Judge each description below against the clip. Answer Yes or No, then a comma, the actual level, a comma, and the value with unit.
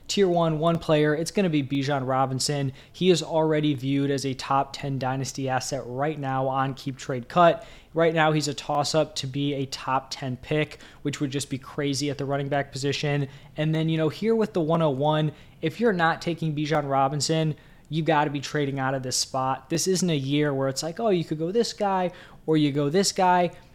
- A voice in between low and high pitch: Yes, medium, 150 Hz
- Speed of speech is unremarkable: No, fast, 225 wpm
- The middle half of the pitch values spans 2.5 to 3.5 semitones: Yes, average, 2.8 semitones